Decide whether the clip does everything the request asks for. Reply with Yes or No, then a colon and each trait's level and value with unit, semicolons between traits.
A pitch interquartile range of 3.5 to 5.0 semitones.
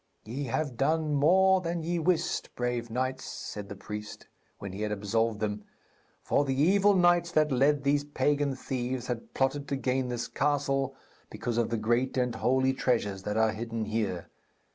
Yes: average, 4.3 semitones